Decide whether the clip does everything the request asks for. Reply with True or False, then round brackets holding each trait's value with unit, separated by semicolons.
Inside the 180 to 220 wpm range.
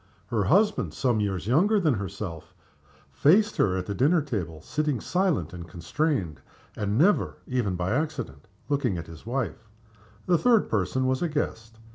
False (155 wpm)